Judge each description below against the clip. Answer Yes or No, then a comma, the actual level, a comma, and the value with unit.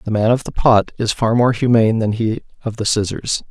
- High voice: No, low, 115 Hz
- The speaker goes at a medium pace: No, fast, 240 wpm